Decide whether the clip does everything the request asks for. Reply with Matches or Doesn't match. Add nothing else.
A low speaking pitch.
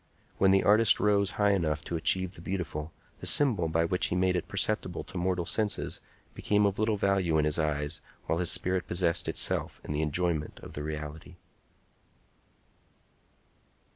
Matches